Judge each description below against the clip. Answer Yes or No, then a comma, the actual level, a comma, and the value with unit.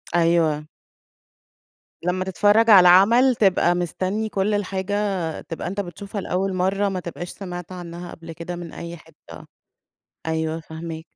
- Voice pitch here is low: No, medium, 180 Hz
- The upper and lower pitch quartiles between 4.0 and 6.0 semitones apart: No, average, 2.7 semitones